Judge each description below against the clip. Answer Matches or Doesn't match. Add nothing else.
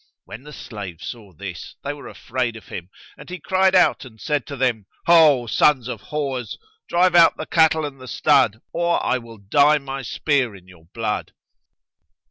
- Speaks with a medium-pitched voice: Doesn't match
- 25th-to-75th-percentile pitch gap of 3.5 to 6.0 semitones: Matches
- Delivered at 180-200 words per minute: Matches